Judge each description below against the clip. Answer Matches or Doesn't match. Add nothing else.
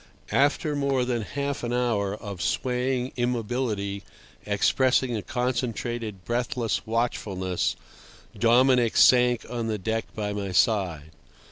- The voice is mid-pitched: Doesn't match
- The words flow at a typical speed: Doesn't match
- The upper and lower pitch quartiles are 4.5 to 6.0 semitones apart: Doesn't match